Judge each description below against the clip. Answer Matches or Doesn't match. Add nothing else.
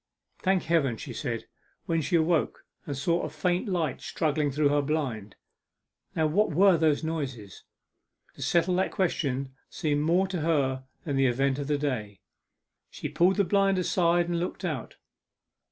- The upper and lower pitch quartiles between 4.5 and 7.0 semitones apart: Doesn't match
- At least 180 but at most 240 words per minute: Doesn't match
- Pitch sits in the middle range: Matches